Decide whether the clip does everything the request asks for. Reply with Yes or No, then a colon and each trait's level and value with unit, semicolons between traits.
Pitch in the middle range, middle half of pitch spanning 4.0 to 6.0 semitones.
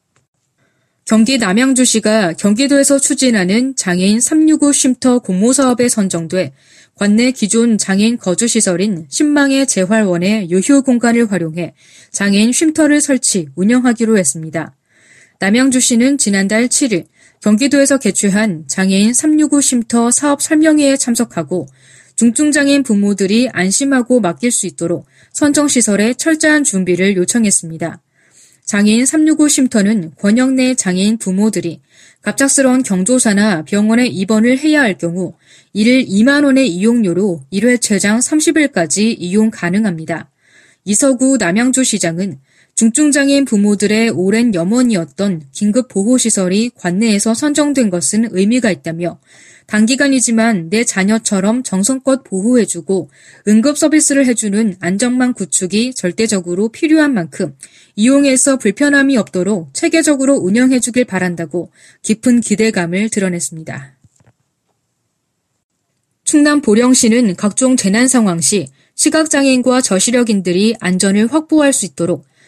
No: high, 220 Hz; wide, 5.4 semitones